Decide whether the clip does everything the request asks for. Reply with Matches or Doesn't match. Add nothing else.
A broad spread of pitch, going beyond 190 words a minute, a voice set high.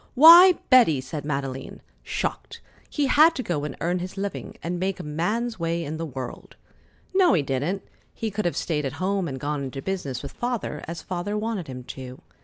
Doesn't match